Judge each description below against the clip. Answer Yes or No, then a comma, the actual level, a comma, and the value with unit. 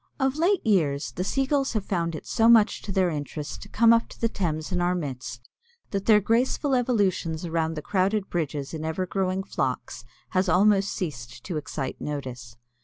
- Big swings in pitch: Yes, wide, 5.8 semitones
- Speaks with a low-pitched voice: No, medium, 180 Hz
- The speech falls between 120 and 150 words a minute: No, average, 190 wpm